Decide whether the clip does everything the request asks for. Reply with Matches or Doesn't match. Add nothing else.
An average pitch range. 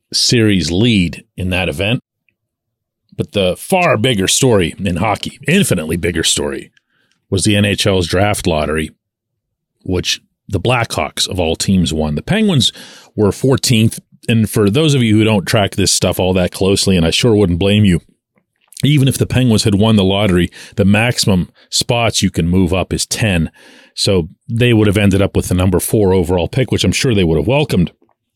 Matches